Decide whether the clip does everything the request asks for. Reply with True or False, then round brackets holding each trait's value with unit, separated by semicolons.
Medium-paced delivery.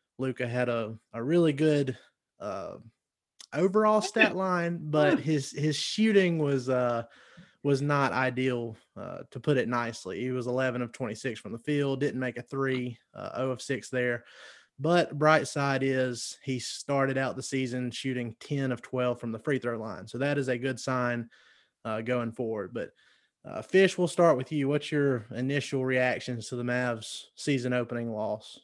True (180 wpm)